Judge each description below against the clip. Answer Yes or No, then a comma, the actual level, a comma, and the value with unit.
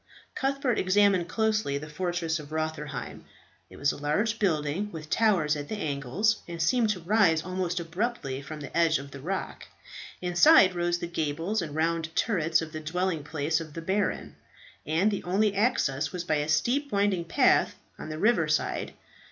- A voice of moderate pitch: Yes, medium, 170 Hz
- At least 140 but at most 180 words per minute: Yes, average, 175 wpm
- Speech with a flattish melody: No, average, 4.6 semitones